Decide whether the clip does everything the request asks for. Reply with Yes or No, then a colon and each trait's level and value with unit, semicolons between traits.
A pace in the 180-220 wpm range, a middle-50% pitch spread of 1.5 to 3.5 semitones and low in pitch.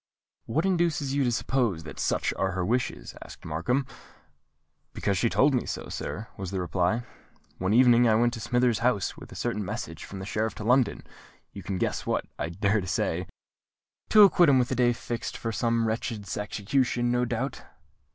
No: average, 185 wpm; average, 4.3 semitones; low, 115 Hz